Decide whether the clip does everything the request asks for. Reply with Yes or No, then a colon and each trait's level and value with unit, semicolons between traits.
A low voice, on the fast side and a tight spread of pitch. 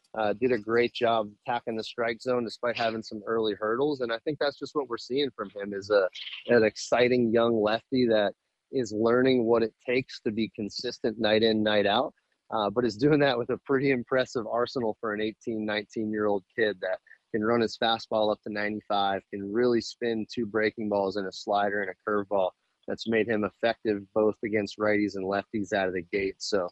Yes: low, 110 Hz; fast, 210 wpm; narrow, 2.3 semitones